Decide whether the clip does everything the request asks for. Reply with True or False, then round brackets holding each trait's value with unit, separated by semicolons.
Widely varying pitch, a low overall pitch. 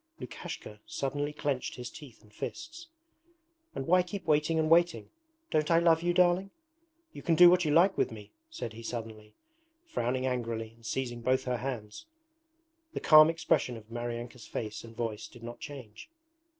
True (6.1 semitones; 130 Hz)